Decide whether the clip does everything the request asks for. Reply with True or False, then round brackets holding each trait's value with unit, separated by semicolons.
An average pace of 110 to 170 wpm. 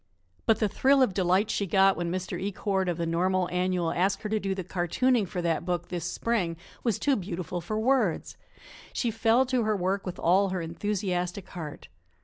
False (195 wpm)